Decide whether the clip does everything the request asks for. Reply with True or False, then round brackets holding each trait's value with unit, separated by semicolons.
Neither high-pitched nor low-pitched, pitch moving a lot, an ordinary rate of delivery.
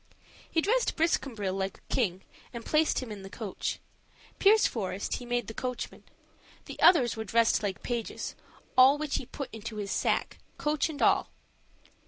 False (240 Hz; 5.8 semitones; 165 wpm)